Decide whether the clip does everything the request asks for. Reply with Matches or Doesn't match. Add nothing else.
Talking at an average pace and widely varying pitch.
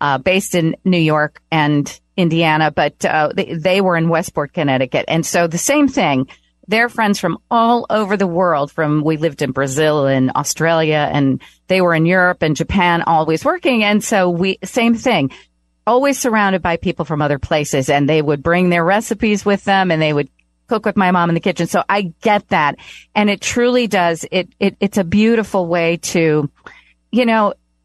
Doesn't match